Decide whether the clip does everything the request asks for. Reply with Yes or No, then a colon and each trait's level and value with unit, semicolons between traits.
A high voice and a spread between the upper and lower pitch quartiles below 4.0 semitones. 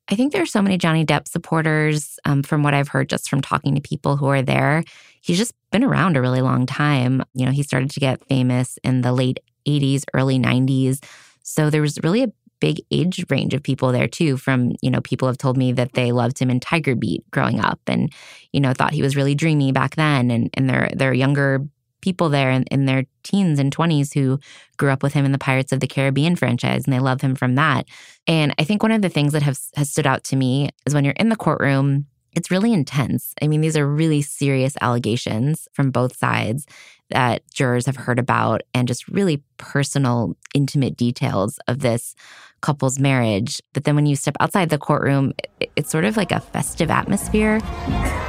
No: medium, 140 Hz; average, 2.9 semitones